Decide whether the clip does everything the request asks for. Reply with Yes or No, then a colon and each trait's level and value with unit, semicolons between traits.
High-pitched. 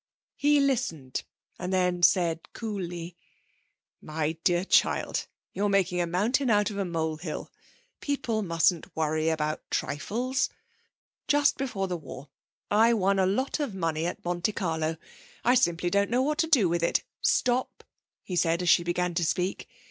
No: medium, 180 Hz